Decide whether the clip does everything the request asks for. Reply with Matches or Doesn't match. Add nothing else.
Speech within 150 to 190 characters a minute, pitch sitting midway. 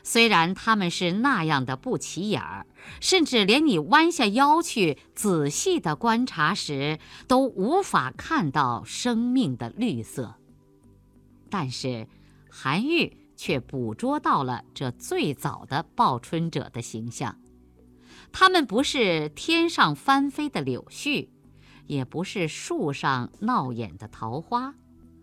Matches